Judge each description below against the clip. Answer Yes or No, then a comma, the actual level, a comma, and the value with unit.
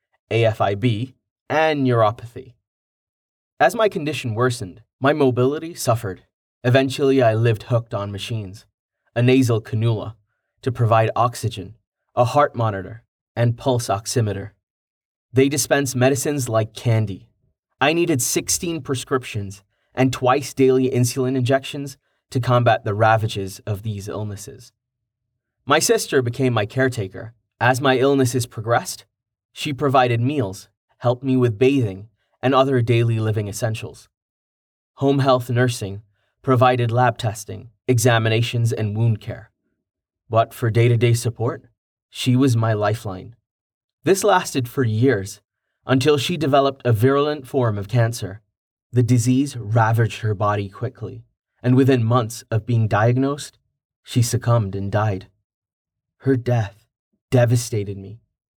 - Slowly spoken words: Yes, slow, 125 wpm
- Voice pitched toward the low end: Yes, low, 120 Hz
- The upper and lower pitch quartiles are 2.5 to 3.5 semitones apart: Yes, average, 3.1 semitones